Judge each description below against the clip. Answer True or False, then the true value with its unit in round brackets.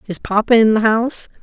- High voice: True (220 Hz)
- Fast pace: True (210 wpm)